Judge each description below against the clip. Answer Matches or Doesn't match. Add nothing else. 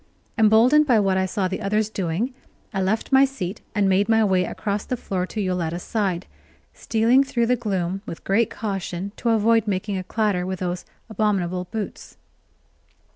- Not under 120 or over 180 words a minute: Matches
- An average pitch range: Matches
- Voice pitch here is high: Matches